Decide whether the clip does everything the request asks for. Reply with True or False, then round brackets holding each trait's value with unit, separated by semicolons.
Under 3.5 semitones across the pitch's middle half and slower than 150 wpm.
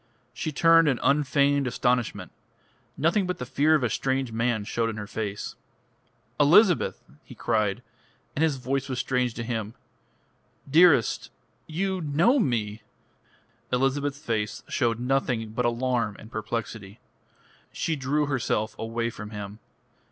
False (4.3 semitones; 135 wpm)